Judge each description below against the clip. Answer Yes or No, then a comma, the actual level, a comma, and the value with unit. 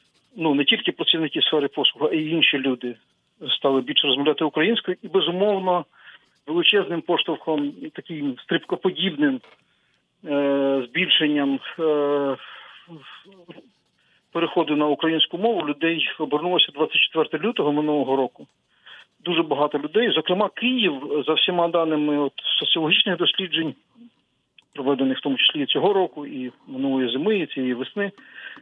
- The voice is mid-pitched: Yes, medium, 160 Hz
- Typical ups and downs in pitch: Yes, average, 4.1 semitones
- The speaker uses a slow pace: No, average, 115 wpm